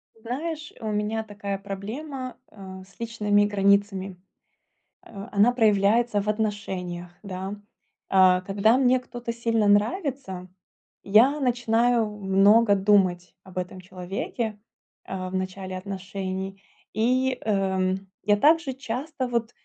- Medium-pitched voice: No, high, 205 Hz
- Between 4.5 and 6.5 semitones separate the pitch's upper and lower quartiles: No, average, 3.6 semitones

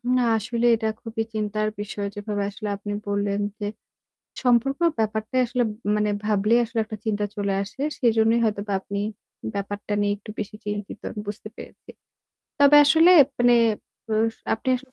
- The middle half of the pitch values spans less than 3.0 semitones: Yes, narrow, 2.4 semitones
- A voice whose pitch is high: Yes, high, 215 Hz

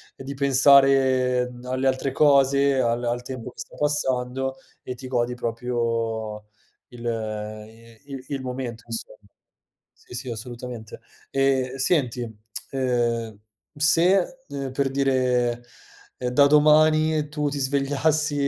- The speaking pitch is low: Yes, low, 130 Hz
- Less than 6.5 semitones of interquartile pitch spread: Yes, average, 2.7 semitones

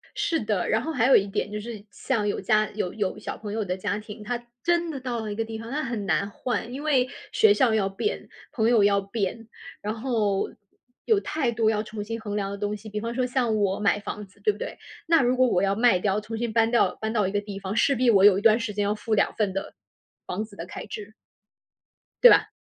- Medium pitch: No, high, 215 Hz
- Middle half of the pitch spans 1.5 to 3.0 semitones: Yes, average, 2.7 semitones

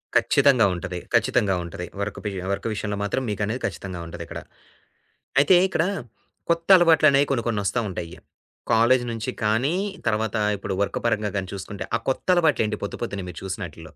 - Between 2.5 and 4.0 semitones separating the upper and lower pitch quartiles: No, average, 4.9 semitones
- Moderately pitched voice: No, low, 105 Hz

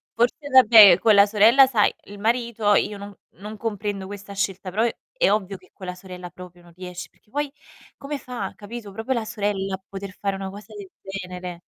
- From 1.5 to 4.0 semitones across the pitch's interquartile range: Yes, average, 2.7 semitones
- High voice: Yes, high, 200 Hz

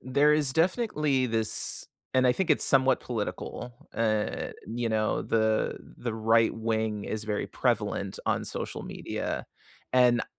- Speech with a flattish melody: No, average, 3.2 semitones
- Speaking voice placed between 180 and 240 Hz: No, low, 120 Hz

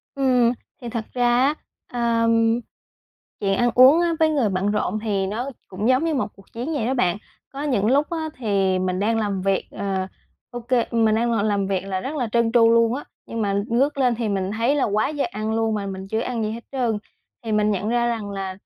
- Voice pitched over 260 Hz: No, high, 230 Hz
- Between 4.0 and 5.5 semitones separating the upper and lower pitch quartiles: No, average, 3.6 semitones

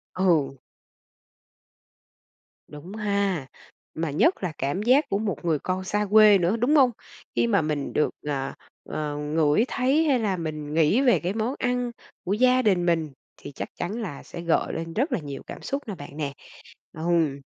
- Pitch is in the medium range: Yes, medium, 180 Hz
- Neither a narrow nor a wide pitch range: No, wide, 6.4 semitones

